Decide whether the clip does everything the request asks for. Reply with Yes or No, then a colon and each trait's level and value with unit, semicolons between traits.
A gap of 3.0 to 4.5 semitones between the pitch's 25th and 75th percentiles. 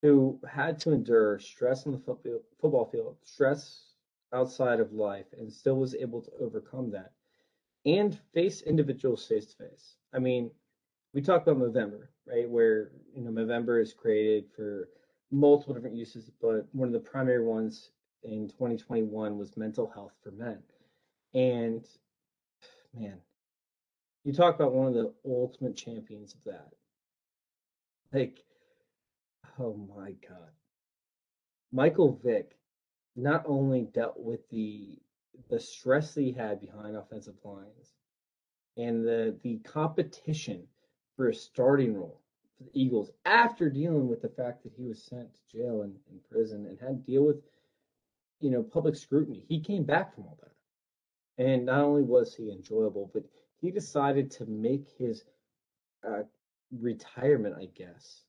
No: average, 4.9 semitones